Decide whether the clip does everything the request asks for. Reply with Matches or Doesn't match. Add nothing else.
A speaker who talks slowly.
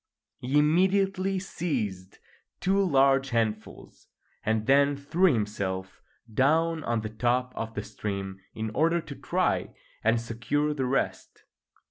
Matches